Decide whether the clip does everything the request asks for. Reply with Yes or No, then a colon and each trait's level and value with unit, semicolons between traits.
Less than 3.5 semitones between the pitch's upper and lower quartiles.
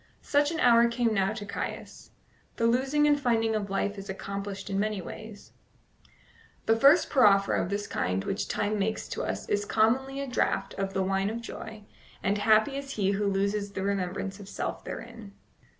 Yes: average, 2.9 semitones